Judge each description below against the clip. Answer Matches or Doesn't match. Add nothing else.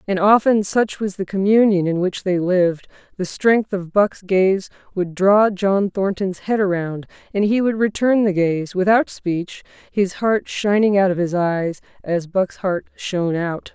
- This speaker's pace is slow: Doesn't match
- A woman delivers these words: Matches